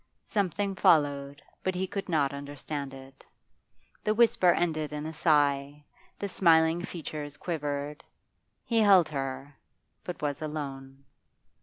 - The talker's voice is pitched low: No, medium, 150 Hz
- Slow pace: Yes, slow, 125 wpm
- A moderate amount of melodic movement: Yes, average, 3.7 semitones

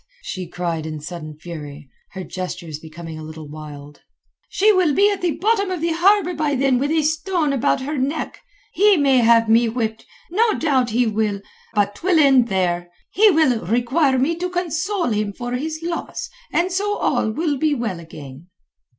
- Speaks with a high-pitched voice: Yes, very high, 255 Hz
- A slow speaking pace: No, average, 185 wpm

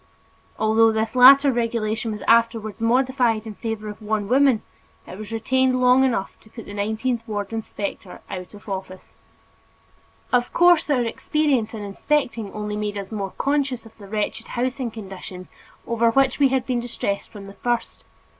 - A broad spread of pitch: No, average, 3.3 semitones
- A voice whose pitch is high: Yes, high, 225 Hz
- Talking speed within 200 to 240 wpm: No, average, 165 wpm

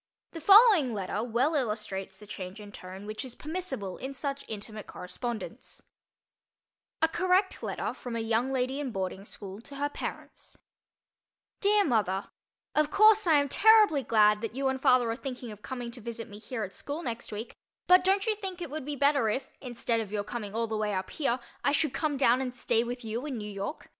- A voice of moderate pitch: No, high, 245 Hz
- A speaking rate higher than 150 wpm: Yes, fast, 205 wpm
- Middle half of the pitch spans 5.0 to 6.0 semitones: Yes, wide, 5.4 semitones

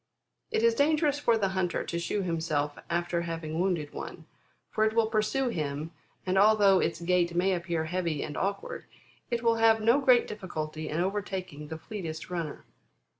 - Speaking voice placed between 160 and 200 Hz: Yes, medium, 185 Hz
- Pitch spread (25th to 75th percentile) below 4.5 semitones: No, average, 4.8 semitones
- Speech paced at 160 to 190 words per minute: Yes, average, 175 wpm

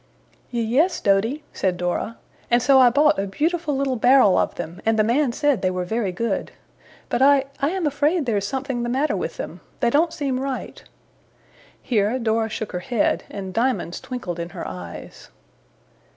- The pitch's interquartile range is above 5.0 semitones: Yes, wide, 5.5 semitones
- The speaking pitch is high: Yes, high, 240 Hz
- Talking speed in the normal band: Yes, average, 180 wpm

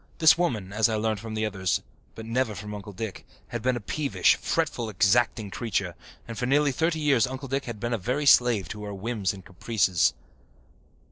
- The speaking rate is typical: Yes, average, 195 wpm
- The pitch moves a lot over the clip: No, average, 3.8 semitones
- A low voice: Yes, low, 115 Hz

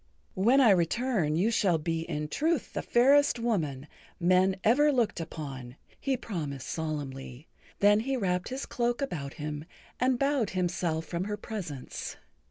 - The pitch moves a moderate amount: No, wide, 7.7 semitones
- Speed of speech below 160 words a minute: Yes, average, 150 wpm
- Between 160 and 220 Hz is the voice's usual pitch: Yes, medium, 185 Hz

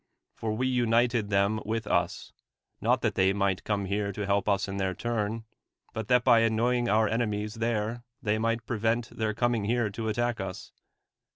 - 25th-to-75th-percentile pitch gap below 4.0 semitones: Yes, narrow, 2.4 semitones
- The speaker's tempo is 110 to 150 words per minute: No, average, 185 wpm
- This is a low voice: Yes, low, 110 Hz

